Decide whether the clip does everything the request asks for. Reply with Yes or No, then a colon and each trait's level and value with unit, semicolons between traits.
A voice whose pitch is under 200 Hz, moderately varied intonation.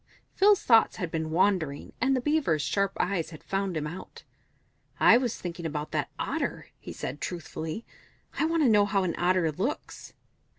No: medium, 185 Hz; wide, 6.0 semitones